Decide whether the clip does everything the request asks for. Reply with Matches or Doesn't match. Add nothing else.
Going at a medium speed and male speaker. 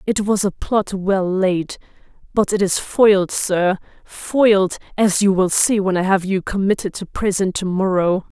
Doesn't match